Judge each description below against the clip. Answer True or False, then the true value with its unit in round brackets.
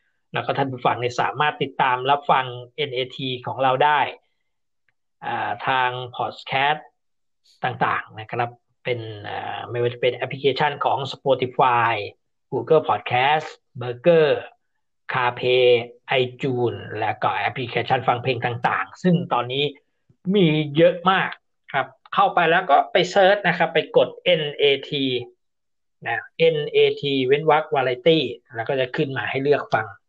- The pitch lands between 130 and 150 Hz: True (135 Hz)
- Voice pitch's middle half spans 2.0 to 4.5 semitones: True (4.1 semitones)